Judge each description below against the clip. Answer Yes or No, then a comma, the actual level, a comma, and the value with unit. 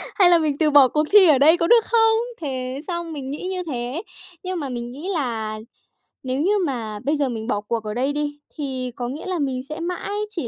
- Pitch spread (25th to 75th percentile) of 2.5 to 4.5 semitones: No, average, 5.2 semitones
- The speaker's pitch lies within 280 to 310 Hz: Yes, very high, 290 Hz